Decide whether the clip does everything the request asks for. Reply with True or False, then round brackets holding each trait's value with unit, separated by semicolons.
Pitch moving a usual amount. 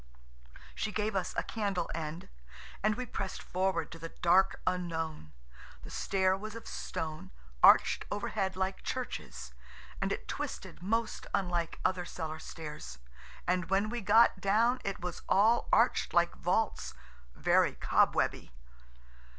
True (3.9 semitones)